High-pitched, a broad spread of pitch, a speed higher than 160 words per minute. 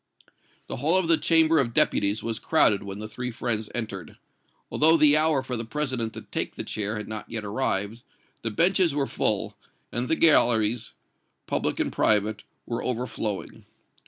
No: low, 120 Hz; wide, 5.7 semitones; average, 170 wpm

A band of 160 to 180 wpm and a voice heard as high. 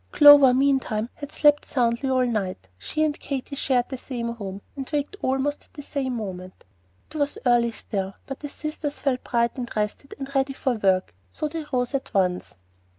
No: average, 190 wpm; very high, 260 Hz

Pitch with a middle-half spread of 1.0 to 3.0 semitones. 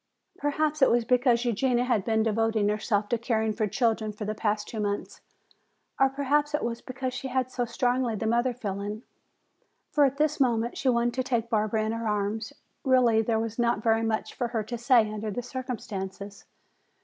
Yes: average, 2.7 semitones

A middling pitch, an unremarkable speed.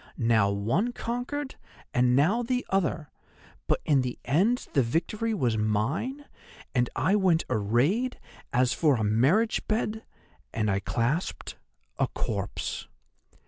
No: medium, 150 Hz; slow, 125 wpm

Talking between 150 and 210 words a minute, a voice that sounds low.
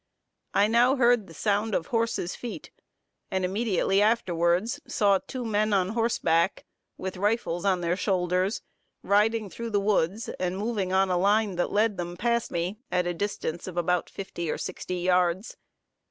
No: average, 165 wpm; high, 195 Hz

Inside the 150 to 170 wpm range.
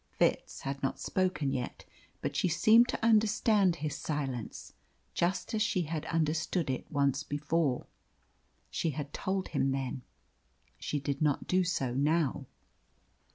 No: average, 140 wpm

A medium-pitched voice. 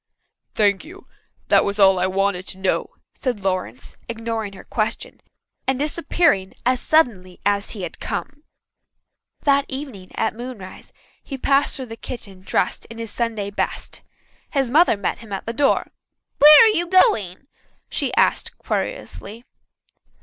No: high, 225 Hz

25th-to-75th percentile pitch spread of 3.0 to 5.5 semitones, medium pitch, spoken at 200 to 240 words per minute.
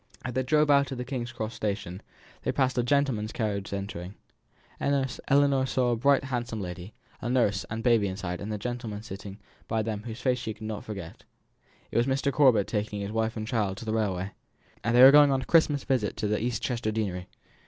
No: average, 4.0 semitones; low, 115 Hz; fast, 205 wpm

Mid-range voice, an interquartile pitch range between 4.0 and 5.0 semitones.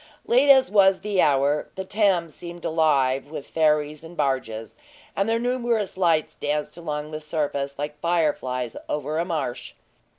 Yes: medium, 155 Hz; average, 4.3 semitones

